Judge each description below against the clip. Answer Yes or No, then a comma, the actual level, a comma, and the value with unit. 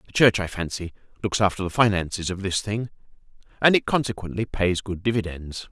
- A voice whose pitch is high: No, low, 100 Hz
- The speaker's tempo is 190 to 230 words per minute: No, average, 180 wpm